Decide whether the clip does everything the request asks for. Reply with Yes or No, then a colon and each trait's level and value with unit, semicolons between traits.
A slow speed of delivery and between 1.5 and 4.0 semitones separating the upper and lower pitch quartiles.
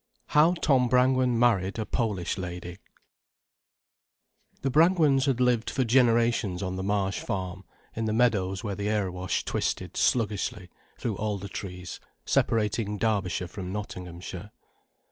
No: slow, 130 wpm; average, 4.6 semitones